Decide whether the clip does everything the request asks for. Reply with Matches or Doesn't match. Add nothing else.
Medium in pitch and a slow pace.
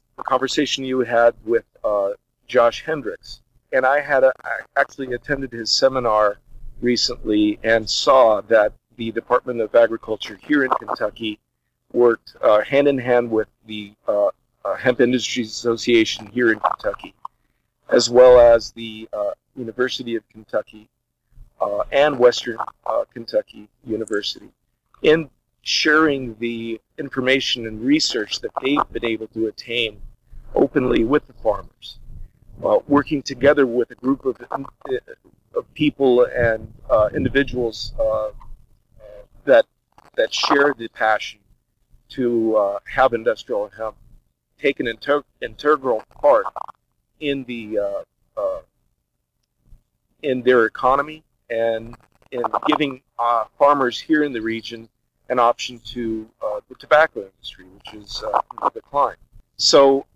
Doesn't match